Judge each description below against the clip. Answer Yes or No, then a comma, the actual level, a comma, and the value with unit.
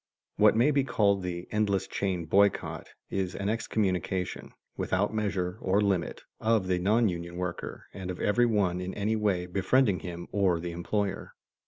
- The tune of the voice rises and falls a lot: No, average, 2.8 semitones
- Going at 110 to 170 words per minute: Yes, average, 165 wpm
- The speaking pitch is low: Yes, very low, 95 Hz